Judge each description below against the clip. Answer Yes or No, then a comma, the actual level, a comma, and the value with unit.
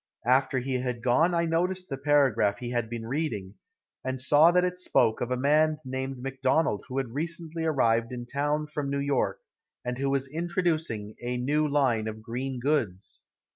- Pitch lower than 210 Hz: Yes, low, 135 Hz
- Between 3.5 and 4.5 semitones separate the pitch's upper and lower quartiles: Yes, average, 3.9 semitones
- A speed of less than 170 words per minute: No, average, 180 wpm